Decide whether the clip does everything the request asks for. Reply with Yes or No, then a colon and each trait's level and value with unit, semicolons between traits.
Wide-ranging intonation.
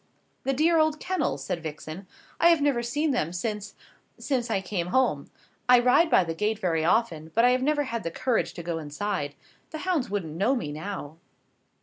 Yes: wide, 8.0 semitones